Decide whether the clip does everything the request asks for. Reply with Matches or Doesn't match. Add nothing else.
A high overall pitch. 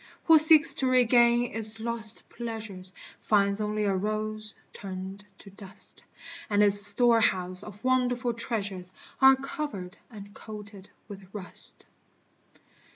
Matches